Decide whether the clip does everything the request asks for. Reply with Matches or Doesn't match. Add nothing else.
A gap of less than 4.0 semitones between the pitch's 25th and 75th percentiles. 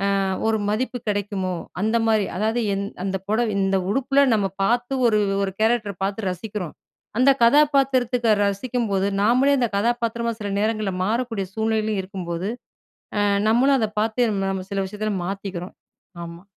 Matches